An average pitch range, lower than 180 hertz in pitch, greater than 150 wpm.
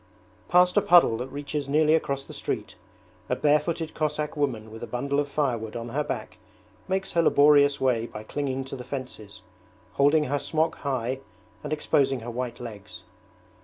Yes: average, 3.5 semitones; medium, 140 Hz; average, 170 wpm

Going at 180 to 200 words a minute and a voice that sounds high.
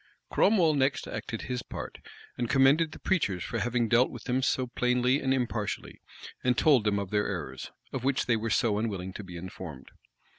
No: average, 185 wpm; low, 120 Hz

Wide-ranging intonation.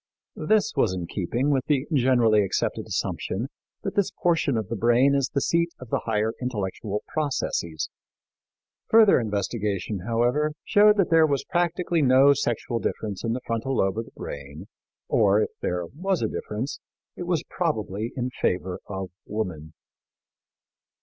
Yes: wide, 6.2 semitones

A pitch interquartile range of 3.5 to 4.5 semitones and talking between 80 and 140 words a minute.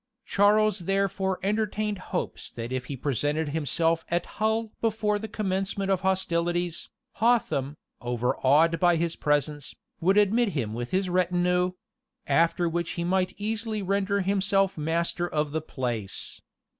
Yes: average, 4.2 semitones; slow, 135 wpm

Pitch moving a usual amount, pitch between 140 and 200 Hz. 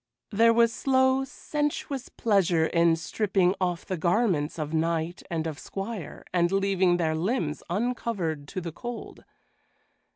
No: wide, 5.8 semitones; medium, 185 Hz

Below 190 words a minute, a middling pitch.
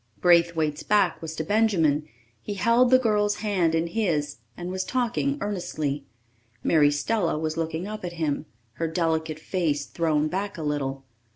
Yes: average, 160 wpm; medium, 165 Hz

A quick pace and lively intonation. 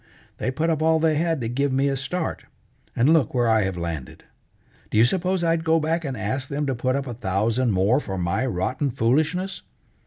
Yes: fast, 215 wpm; wide, 6.0 semitones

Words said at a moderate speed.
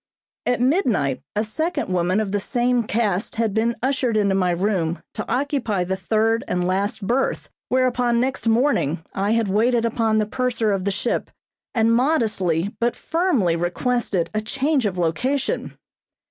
Yes: average, 160 wpm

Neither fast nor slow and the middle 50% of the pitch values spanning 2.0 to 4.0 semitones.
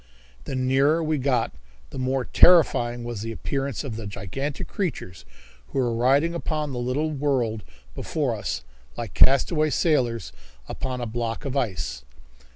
Yes: average, 150 wpm; average, 3.7 semitones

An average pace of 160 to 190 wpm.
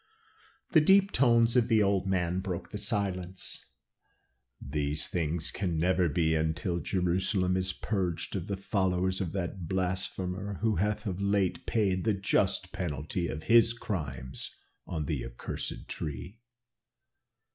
No: slow, 135 wpm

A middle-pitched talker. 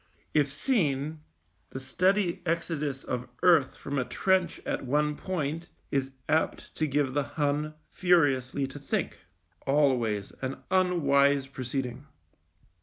Yes: medium, 145 Hz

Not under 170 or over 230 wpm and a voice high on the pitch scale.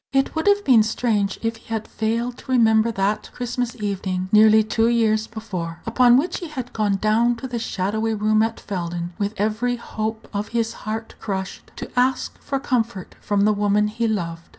Yes: average, 190 wpm; high, 220 Hz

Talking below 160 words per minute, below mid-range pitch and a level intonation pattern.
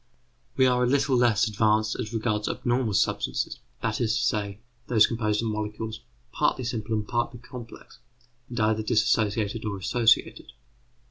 Yes: average, 150 wpm; low, 110 Hz; narrow, 2.0 semitones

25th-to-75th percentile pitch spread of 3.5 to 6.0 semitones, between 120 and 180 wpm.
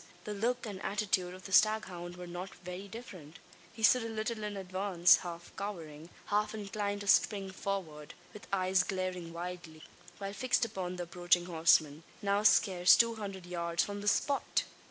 No: average, 2.8 semitones; average, 170 wpm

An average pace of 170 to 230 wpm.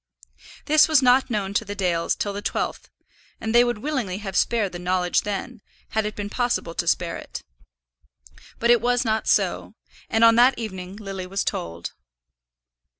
Yes: average, 175 wpm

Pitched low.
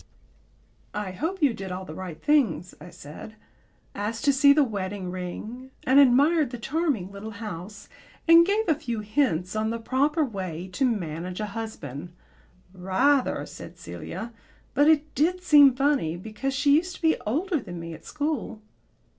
No: high, 230 Hz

